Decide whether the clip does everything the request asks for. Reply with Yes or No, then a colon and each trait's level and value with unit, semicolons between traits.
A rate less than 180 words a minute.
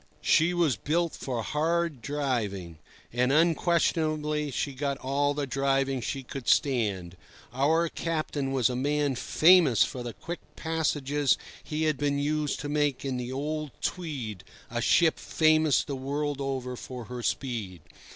Yes: average, 150 wpm